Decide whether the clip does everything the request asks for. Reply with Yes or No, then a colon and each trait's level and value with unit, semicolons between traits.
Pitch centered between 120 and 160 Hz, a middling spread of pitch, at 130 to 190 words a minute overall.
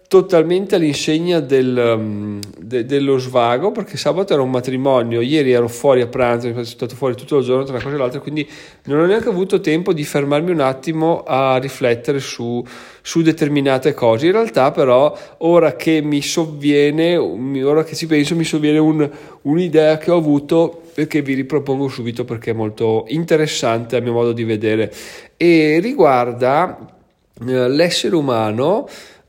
Yes: medium, 140 Hz; average, 4.3 semitones; average, 165 wpm